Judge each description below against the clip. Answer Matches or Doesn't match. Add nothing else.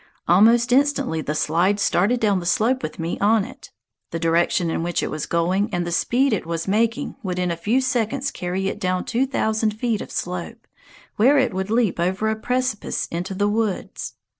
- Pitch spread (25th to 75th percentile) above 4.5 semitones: Matches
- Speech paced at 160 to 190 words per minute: Doesn't match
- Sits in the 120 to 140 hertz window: Doesn't match